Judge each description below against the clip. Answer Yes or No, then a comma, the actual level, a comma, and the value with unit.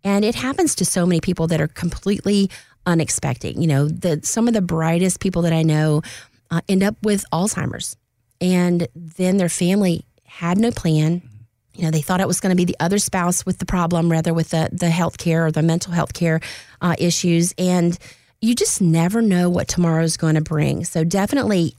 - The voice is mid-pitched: Yes, medium, 170 Hz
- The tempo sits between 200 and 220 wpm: Yes, fast, 205 wpm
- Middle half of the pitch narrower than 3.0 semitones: Yes, narrow, 2.5 semitones